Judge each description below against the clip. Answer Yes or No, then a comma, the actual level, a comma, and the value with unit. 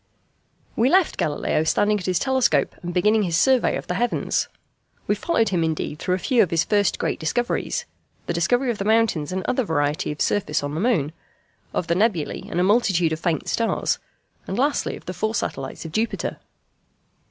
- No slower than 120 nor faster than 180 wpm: No, average, 195 wpm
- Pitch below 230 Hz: Yes, high, 190 Hz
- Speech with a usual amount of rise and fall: No, wide, 5.8 semitones